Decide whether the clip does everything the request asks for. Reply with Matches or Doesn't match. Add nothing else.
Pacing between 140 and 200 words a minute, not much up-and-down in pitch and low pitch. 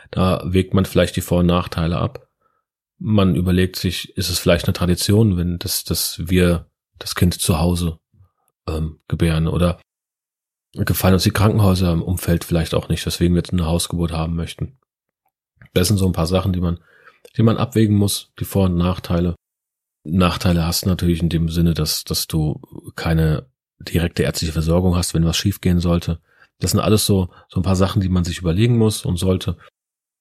Matches